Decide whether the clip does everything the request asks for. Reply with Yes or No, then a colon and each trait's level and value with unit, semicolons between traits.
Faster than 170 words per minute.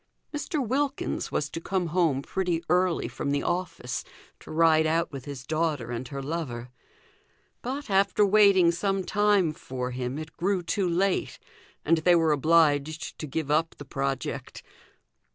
No: average, 155 wpm